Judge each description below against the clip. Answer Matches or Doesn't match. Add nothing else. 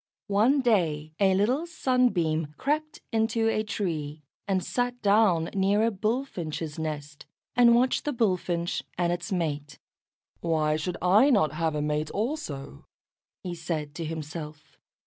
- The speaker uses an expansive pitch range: Matches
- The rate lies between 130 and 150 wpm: Matches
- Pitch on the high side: Doesn't match